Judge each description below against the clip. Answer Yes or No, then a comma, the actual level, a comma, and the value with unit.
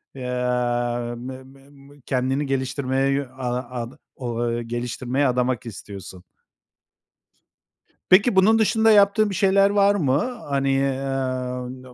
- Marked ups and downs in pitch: No, narrow, 2.4 semitones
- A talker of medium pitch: No, low, 130 Hz